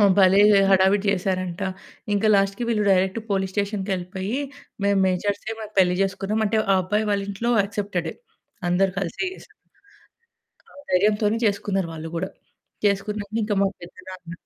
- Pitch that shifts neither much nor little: No, narrow, 1.7 semitones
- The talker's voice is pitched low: No, high, 195 Hz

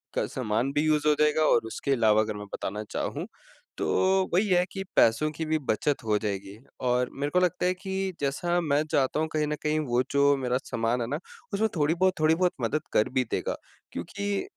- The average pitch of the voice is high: No, medium, 145 Hz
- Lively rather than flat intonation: Yes, wide, 6.4 semitones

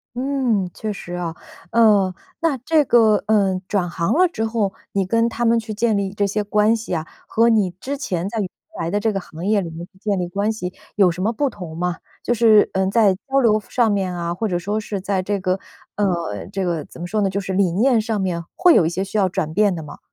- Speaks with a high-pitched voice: Yes, high, 200 Hz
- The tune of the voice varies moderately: Yes, average, 3.5 semitones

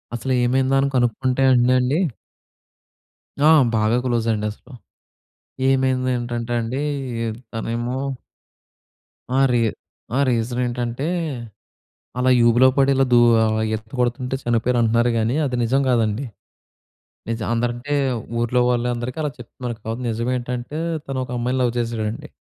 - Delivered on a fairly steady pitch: Yes, narrow, 1.7 semitones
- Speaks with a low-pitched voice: Yes, low, 120 Hz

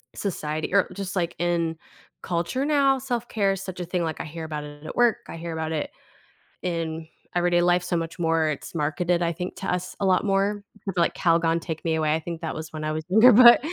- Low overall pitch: No, medium, 170 Hz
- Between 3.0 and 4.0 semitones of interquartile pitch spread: Yes, average, 3.3 semitones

